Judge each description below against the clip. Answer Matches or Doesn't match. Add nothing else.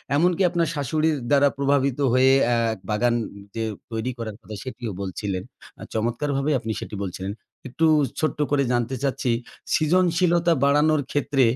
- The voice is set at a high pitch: Doesn't match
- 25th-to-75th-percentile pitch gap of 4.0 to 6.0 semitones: Matches